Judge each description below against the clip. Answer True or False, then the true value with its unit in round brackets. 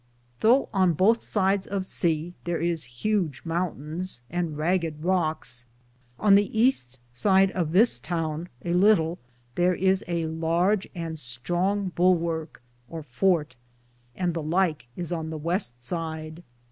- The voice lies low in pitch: False (170 Hz)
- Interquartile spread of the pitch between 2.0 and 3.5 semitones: True (3.0 semitones)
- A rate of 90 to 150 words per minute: True (135 wpm)